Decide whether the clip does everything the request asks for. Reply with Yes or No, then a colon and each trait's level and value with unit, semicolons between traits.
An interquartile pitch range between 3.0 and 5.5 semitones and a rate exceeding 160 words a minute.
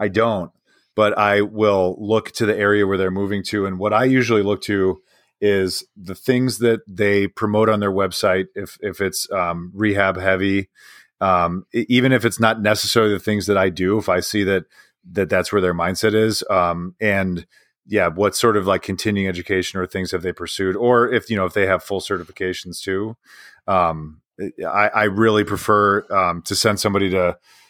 No: narrow, 2.4 semitones; average, 195 wpm